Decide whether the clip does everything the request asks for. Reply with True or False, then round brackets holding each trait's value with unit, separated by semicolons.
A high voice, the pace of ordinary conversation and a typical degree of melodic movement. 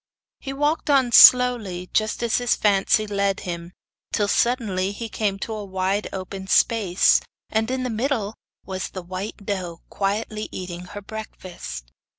True (205 Hz; 155 wpm; 3.3 semitones)